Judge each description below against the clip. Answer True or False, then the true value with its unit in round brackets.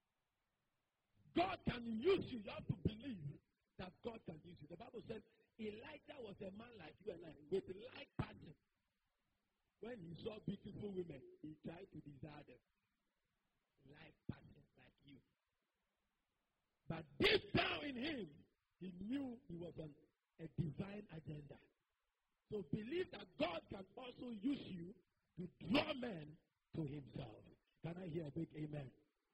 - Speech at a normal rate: True (150 wpm)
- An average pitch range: False (6.9 semitones)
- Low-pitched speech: False (180 Hz)